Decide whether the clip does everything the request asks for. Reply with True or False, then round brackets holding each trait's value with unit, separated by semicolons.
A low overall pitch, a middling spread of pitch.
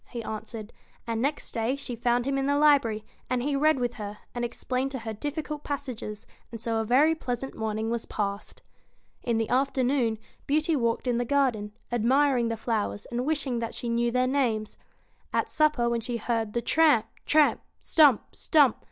False (240 Hz; 3.6 semitones)